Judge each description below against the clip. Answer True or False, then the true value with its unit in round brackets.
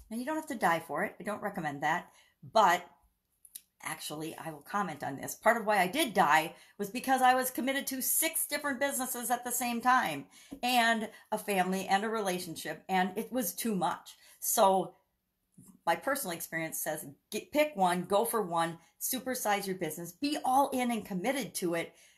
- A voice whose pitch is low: False (215 Hz)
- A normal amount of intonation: False (6.3 semitones)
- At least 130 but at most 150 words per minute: False (190 wpm)